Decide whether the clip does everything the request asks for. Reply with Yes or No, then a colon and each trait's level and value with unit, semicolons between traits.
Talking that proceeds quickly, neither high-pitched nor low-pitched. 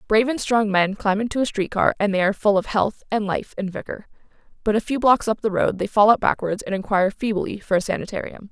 No: fast, 255 wpm; high, 210 Hz